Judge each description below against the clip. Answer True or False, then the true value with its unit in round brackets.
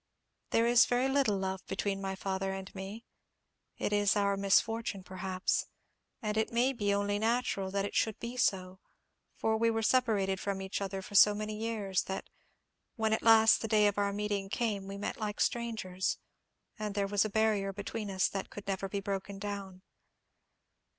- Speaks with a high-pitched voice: True (205 Hz)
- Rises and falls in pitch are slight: True (2.2 semitones)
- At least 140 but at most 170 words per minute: False (185 wpm)